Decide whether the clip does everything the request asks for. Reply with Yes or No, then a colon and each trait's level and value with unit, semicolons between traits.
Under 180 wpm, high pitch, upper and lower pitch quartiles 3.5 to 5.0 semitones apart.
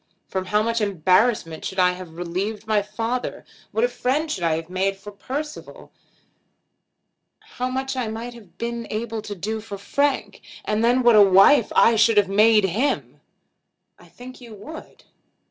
Yes: average, 170 wpm; high, 215 Hz; average, 3.8 semitones